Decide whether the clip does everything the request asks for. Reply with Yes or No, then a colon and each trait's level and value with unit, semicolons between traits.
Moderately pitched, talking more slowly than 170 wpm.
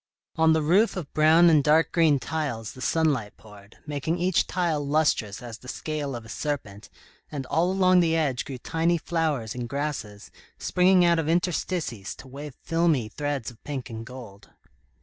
No: medium, 150 Hz; average, 175 wpm